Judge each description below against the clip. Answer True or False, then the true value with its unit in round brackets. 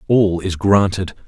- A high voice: False (95 Hz)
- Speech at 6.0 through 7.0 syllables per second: False (4.0 syllables/s)